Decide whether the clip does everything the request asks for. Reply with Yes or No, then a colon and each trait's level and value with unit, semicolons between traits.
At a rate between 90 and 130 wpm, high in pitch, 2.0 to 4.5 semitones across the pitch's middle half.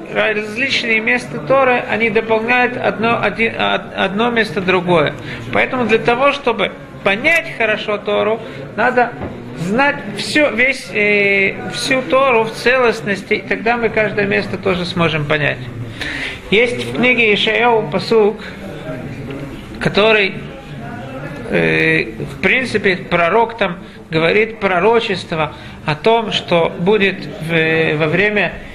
No: average, 115 wpm; high, 210 Hz; average, 5.3 semitones